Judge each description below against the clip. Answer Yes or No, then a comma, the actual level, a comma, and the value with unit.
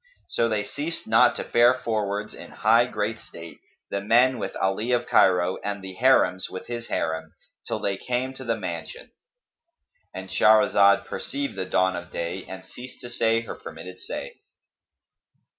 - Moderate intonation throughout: Yes, average, 4.6 semitones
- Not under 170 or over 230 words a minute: No, average, 160 wpm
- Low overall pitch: Yes, low, 110 Hz